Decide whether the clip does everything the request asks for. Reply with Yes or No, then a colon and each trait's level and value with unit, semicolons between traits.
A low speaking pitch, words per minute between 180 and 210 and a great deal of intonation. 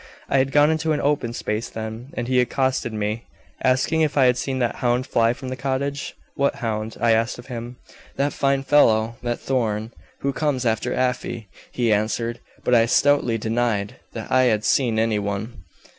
No: low, 120 Hz; average, 190 wpm; average, 2.9 semitones